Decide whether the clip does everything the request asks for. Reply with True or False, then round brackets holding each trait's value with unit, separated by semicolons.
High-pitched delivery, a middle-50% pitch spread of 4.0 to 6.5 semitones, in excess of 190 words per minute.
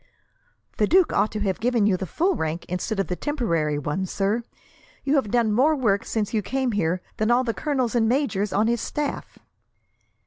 True (220 Hz; 4.8 semitones; 200 wpm)